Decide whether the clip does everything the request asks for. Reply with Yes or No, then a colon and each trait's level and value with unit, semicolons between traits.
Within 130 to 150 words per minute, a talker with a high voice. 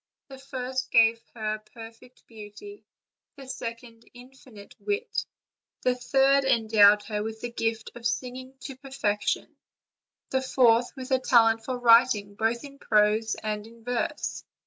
Yes: average, 140 wpm; high, 235 Hz